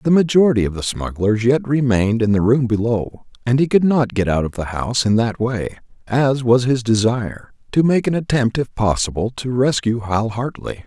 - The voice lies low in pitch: Yes, low, 120 Hz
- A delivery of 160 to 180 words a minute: No, fast, 205 wpm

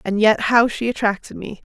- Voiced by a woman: Yes, female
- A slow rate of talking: No, fast, 210 wpm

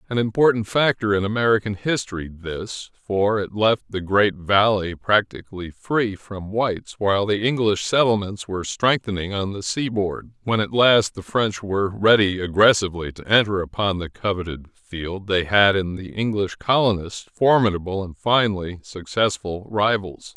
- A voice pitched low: Yes, low, 100 Hz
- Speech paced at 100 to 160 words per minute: Yes, average, 150 wpm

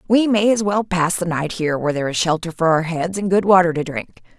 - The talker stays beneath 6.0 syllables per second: No, 6.1 syllables/s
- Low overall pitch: No, medium, 175 Hz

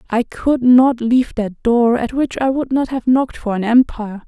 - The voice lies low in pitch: No, high, 245 Hz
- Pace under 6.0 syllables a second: Yes, 5.1 syllables/s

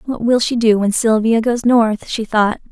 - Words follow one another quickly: Yes, fast, 220 wpm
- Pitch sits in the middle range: No, high, 225 Hz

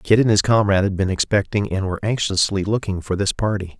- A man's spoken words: Yes, male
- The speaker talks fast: Yes, fast, 220 wpm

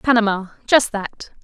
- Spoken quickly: No, slow, 125 wpm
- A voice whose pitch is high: Yes, high, 220 Hz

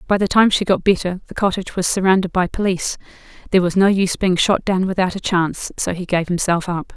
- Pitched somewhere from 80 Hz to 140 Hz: No, medium, 185 Hz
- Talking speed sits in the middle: No, fast, 235 wpm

